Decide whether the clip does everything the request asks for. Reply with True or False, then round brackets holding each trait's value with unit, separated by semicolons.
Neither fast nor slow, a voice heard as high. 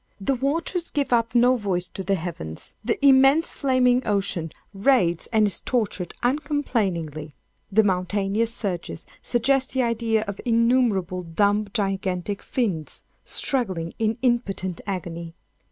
False (125 wpm; 210 Hz)